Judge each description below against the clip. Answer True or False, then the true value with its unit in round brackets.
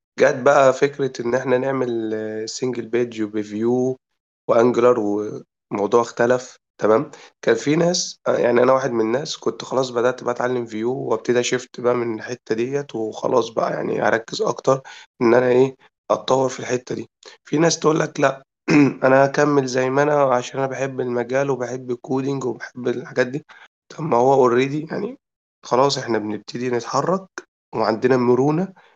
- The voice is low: True (125 Hz)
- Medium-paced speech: False (155 wpm)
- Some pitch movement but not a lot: False (2.2 semitones)